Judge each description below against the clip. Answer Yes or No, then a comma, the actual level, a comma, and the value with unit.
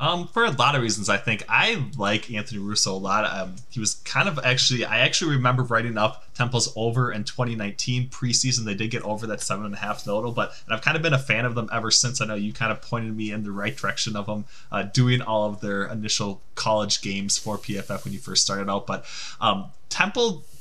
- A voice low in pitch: Yes, low, 110 Hz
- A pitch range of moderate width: Yes, average, 3.2 semitones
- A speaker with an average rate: No, fast, 240 wpm